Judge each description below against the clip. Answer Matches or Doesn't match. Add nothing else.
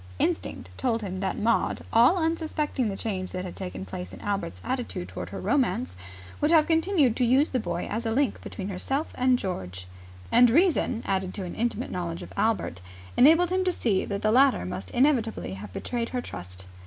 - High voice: Matches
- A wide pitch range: Matches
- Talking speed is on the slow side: Doesn't match